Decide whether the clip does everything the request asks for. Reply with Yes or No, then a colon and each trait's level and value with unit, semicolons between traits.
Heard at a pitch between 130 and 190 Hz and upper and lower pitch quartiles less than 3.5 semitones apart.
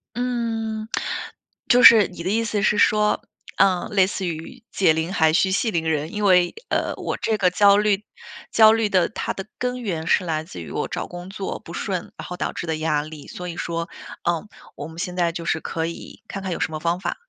No: medium, 185 Hz; average, 4.0 semitones